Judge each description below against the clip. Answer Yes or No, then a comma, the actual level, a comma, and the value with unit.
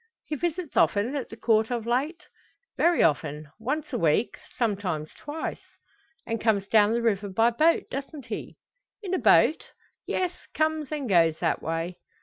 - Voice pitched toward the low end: No, high, 235 Hz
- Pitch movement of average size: No, wide, 7.3 semitones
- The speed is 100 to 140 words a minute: No, average, 160 wpm